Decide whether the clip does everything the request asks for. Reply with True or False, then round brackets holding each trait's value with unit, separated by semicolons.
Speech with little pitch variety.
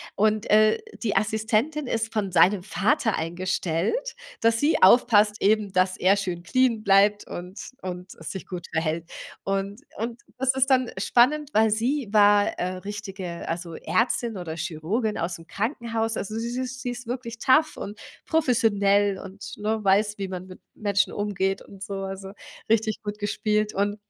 False (3.1 semitones)